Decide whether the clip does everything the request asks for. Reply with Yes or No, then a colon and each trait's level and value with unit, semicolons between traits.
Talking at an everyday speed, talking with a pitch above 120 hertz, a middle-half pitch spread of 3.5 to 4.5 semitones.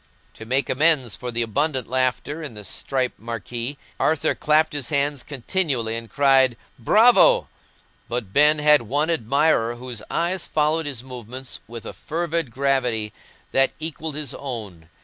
Yes: average, 150 wpm; low, 135 Hz; average, 4.2 semitones